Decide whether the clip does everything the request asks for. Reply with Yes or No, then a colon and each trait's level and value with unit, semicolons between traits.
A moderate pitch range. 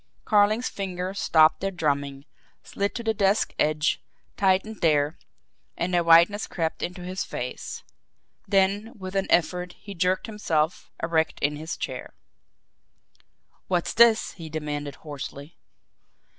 Yes: average, 4.0 semitones